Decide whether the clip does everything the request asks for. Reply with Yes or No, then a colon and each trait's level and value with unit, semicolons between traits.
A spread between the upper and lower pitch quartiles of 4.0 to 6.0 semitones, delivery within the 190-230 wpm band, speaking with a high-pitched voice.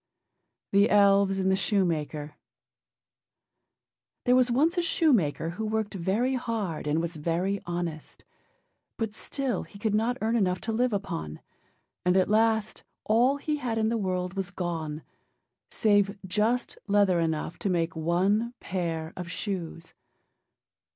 No: average, 4.5 semitones; average, 140 wpm; high, 195 Hz